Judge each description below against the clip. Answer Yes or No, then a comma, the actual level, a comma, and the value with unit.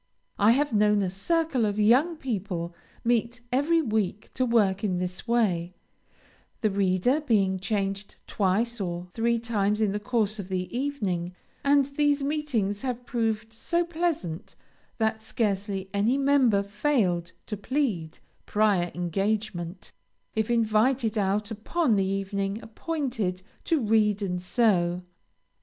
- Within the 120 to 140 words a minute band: Yes, slow, 135 wpm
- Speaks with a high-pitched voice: Yes, high, 215 Hz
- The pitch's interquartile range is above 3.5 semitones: Yes, average, 4.1 semitones